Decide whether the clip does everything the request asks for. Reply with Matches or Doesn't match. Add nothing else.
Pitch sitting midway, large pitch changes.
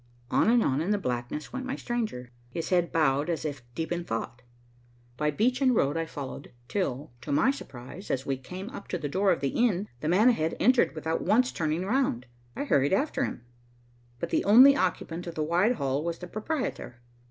Matches